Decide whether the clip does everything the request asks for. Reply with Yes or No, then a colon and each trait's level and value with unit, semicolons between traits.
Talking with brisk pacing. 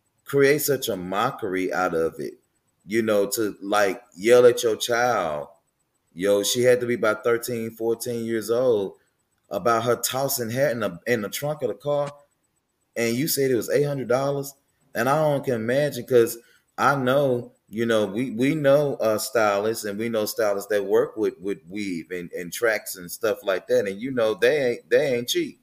No: average, 195 wpm